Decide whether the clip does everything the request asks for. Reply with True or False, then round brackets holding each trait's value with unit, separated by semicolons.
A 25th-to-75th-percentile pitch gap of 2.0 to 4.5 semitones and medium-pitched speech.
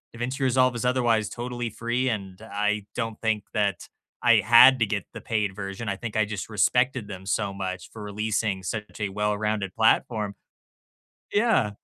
False (2.7 semitones; 110 Hz)